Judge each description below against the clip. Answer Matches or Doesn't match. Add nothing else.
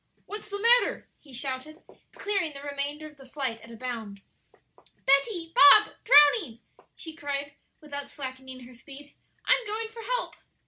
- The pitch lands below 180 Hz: Doesn't match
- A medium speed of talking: Matches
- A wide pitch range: Matches